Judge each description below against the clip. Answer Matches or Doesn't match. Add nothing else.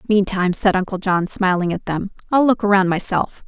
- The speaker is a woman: Matches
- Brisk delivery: Doesn't match